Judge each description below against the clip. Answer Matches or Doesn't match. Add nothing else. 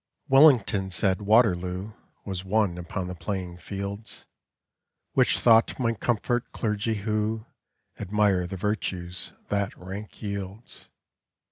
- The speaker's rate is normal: Doesn't match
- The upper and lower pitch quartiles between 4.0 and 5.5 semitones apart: Doesn't match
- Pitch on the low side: Matches